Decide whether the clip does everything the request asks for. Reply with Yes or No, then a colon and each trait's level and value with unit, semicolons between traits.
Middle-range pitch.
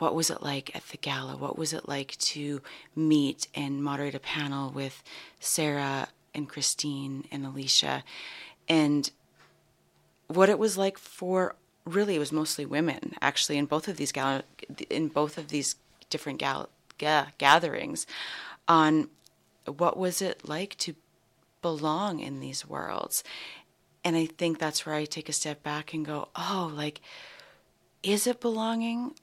Yes: medium, 155 Hz